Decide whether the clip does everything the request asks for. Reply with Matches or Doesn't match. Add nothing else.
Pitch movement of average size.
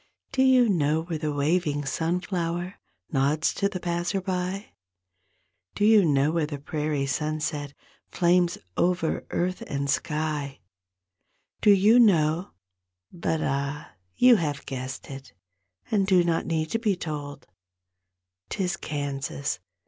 Matches